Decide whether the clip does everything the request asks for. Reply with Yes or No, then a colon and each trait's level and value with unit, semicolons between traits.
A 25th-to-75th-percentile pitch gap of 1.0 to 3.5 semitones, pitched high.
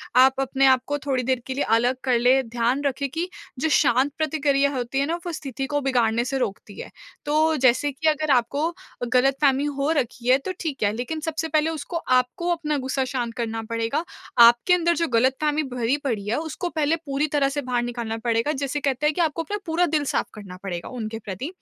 No: average, 3.9 semitones; very high, 270 Hz